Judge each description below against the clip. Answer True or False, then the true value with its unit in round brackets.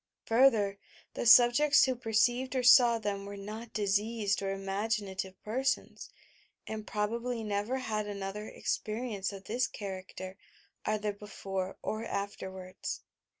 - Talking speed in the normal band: False (125 wpm)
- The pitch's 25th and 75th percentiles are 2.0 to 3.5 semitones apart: True (2.9 semitones)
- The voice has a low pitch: False (210 Hz)